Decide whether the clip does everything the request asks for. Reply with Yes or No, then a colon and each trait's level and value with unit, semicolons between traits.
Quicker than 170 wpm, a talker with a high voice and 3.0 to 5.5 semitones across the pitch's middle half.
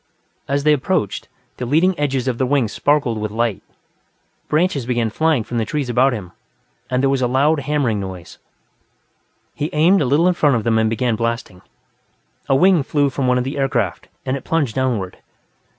No: average, 190 wpm; low, 130 Hz; average, 4.0 semitones